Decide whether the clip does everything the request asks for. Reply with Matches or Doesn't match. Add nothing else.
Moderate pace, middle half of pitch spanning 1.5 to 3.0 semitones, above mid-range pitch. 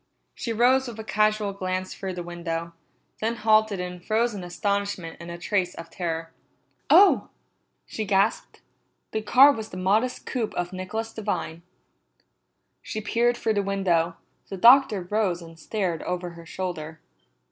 Doesn't match